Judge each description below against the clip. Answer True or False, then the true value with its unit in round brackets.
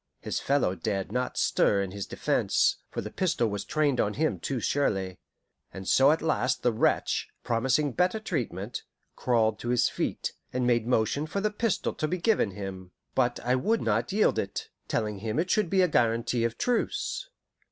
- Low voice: True (125 Hz)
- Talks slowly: False (185 wpm)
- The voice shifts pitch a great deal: True (6.7 semitones)